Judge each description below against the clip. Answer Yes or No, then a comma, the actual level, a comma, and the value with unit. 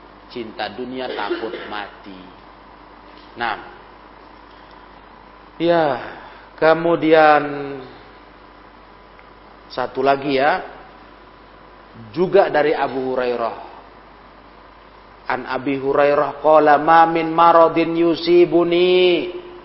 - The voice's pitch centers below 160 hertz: Yes, medium, 140 Hz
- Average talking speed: No, slow, 65 wpm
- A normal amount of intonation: No, wide, 8.6 semitones